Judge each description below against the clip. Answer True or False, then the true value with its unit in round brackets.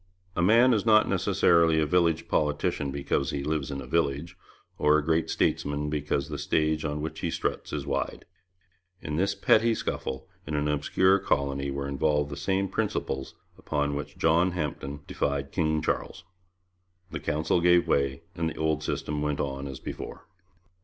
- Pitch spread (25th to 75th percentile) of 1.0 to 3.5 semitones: True (2.8 semitones)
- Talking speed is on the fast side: False (170 wpm)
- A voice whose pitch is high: False (75 Hz)